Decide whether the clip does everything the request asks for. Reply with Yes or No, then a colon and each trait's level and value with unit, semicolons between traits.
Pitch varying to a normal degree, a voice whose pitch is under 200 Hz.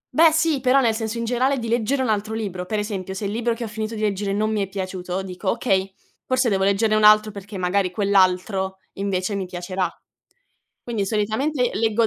No: average, 3.1 semitones; high, 210 Hz